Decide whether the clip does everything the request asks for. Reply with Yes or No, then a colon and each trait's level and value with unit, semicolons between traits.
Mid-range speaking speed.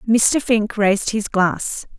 Yes: average, 150 wpm